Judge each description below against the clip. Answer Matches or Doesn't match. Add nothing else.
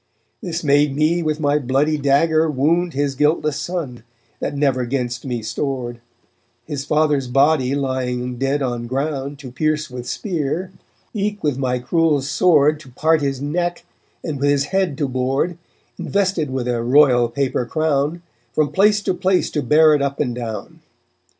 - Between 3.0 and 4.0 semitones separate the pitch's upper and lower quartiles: Matches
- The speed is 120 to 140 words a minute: Doesn't match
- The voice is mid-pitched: Matches